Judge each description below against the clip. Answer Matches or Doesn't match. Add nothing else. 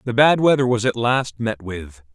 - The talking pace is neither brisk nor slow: Doesn't match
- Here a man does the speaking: Matches